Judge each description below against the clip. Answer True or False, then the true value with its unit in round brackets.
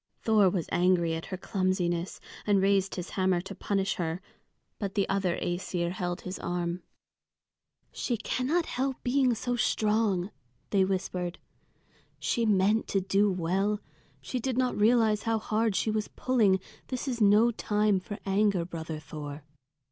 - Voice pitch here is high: True (195 Hz)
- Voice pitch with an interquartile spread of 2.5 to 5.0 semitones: True (3.4 semitones)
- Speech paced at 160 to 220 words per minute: False (150 wpm)